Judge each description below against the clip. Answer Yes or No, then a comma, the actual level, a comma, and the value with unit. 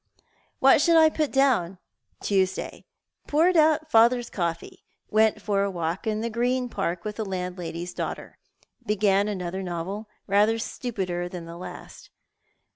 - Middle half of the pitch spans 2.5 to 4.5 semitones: No, average, 5.0 semitones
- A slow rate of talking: No, average, 145 wpm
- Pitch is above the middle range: Yes, high, 205 Hz